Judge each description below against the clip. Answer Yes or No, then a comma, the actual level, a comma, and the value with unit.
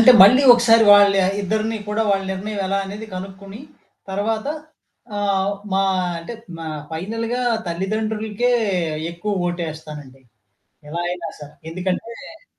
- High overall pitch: Yes, high, 200 Hz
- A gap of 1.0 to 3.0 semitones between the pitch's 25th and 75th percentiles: No, average, 3.6 semitones